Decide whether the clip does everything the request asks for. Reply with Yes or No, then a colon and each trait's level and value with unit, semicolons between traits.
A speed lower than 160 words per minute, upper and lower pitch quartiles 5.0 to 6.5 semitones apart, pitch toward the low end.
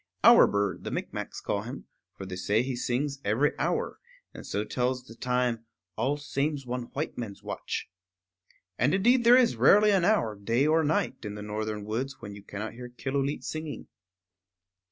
No: average, 175 wpm; wide, 5.4 semitones; low, 125 Hz